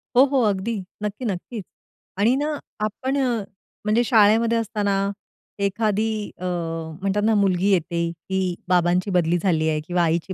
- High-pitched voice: Yes, high, 195 Hz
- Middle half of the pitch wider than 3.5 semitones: Yes, average, 4.1 semitones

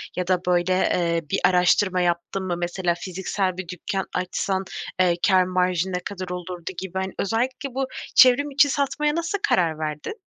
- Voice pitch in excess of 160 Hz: Yes, medium, 185 Hz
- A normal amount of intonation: No, narrow, 2.1 semitones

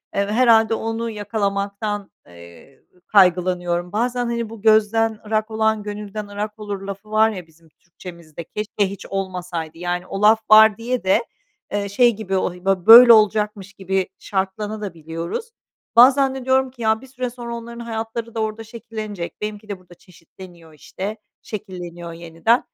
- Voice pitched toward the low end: No, high, 210 Hz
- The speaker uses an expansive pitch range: No, average, 3.4 semitones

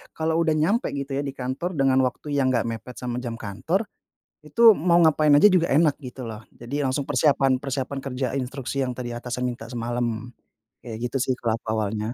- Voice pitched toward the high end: No, low, 130 Hz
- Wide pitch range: No, average, 3.3 semitones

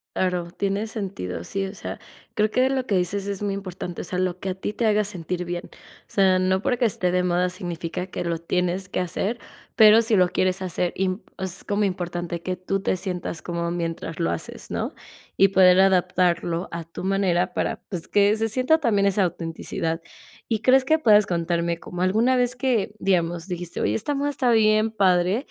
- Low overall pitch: No, medium, 185 Hz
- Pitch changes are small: No, average, 3.1 semitones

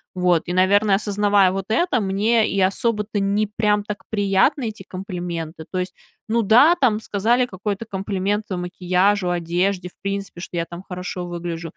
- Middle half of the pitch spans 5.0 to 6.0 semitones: No, narrow, 2.6 semitones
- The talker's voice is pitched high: Yes, high, 195 Hz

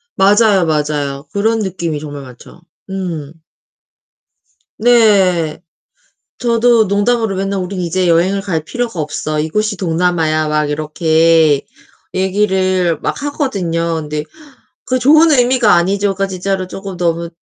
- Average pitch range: Yes, average, 4.3 semitones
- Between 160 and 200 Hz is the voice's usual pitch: Yes, medium, 185 Hz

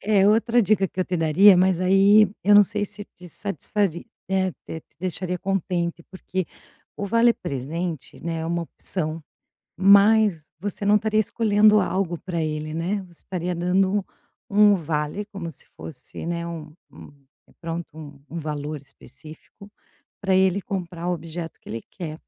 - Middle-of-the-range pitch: Yes, medium, 180 Hz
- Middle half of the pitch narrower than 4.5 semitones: Yes, average, 3.5 semitones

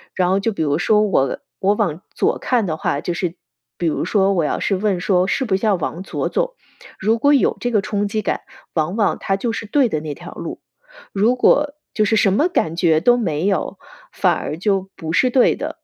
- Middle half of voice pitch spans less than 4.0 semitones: No, average, 4.3 semitones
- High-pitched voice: Yes, high, 195 Hz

